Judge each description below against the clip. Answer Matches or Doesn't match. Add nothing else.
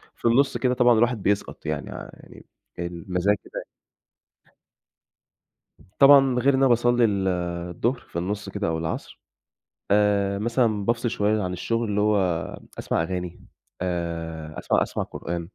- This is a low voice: Matches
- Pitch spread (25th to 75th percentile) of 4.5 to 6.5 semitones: Matches